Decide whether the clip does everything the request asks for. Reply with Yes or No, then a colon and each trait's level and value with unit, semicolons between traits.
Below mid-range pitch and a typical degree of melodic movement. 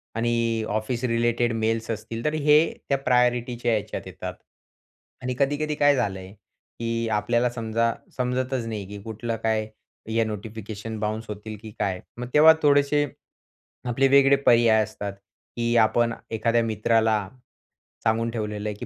No: low, 115 Hz; narrow, 2.1 semitones